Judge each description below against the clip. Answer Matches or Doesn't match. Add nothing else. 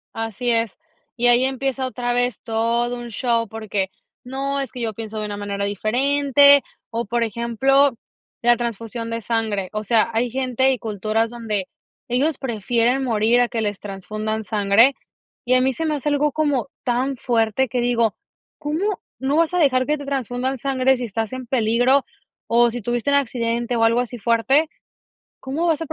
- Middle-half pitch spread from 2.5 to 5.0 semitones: Matches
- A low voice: Doesn't match